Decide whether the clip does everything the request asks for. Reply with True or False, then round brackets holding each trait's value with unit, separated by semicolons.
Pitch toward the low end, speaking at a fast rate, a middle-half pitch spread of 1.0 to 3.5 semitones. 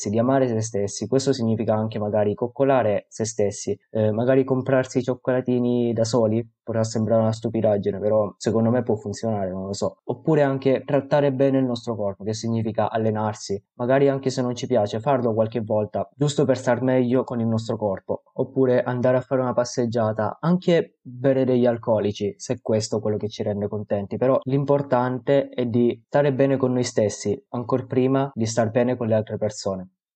True (120 Hz; 185 wpm; 3.2 semitones)